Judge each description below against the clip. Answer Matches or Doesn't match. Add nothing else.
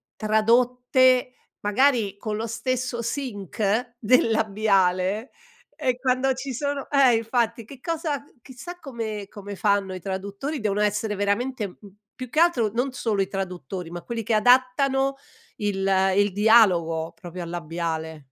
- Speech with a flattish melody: Doesn't match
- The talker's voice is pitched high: Matches